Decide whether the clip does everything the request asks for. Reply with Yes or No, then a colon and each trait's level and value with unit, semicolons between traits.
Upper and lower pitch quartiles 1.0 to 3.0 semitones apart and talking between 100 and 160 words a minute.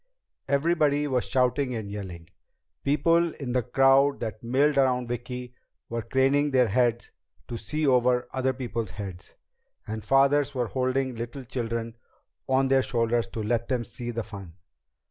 Yes: average, 2.7 semitones; average, 150 wpm